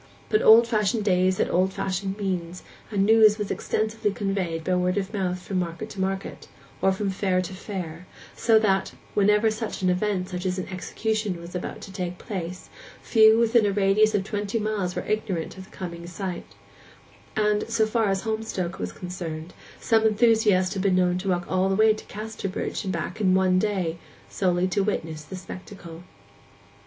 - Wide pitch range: No, average, 2.7 semitones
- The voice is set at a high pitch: Yes, high, 195 Hz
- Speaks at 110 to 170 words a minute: No, average, 185 wpm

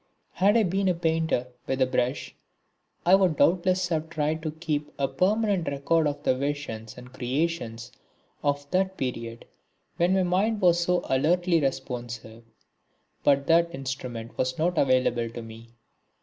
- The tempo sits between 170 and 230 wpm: No, average, 150 wpm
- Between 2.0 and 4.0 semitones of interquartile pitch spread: No, wide, 5.5 semitones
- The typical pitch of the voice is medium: Yes, medium, 150 Hz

